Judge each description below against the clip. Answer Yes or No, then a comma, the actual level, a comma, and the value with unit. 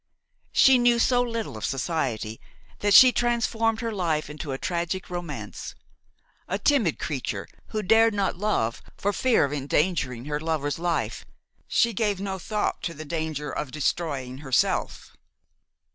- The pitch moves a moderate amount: No, wide, 6.9 semitones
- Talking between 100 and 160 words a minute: Yes, average, 145 wpm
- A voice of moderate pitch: Yes, medium, 175 Hz